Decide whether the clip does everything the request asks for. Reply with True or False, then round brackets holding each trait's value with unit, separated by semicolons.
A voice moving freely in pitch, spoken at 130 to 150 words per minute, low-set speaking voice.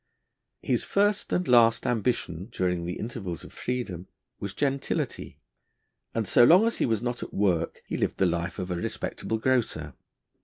False (5.7 semitones; 165 wpm; 110 Hz)